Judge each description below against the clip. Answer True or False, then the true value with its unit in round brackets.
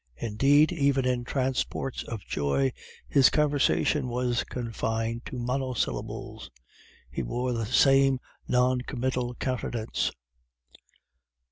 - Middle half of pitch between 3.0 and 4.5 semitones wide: False (2.4 semitones)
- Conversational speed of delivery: False (100 wpm)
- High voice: False (125 Hz)